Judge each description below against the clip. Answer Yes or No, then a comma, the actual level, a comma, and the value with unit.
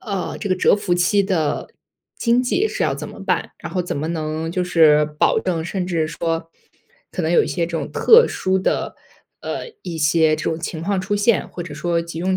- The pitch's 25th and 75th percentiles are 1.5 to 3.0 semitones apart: Yes, average, 2.7 semitones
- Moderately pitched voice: Yes, medium, 175 Hz